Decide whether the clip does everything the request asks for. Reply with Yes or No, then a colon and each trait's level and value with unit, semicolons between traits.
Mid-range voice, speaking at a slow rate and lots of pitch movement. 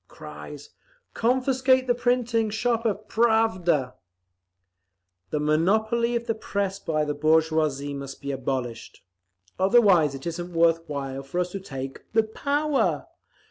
Yes: medium, 180 Hz; slow, 130 wpm; wide, 7.6 semitones